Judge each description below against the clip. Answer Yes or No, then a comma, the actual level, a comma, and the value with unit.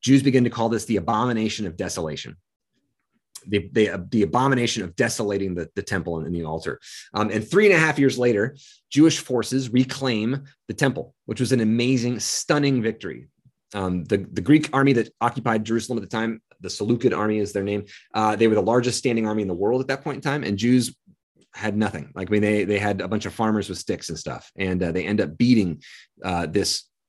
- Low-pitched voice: Yes, low, 110 Hz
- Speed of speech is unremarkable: No, fast, 215 wpm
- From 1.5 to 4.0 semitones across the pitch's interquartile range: Yes, average, 3.7 semitones